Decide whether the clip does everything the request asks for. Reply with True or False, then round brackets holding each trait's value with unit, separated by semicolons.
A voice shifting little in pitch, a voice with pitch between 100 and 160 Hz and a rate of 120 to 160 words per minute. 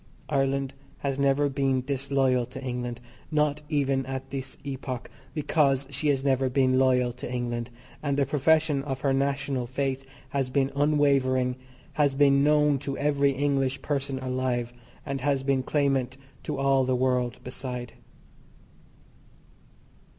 True (1.5 semitones; 135 Hz; 140 wpm)